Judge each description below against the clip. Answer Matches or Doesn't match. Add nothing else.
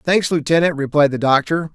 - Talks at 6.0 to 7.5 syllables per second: Doesn't match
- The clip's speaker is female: Doesn't match